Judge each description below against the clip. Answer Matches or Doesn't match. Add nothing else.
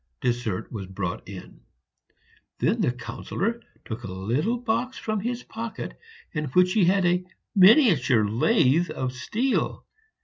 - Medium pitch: Matches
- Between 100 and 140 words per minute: Matches